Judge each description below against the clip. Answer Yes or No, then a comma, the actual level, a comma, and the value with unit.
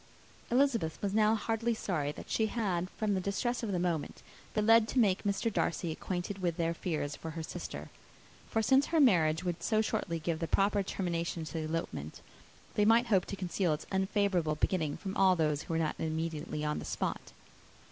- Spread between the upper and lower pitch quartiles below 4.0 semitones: No, average, 4.6 semitones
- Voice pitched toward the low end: No, medium, 185 Hz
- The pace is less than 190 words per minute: No, average, 200 wpm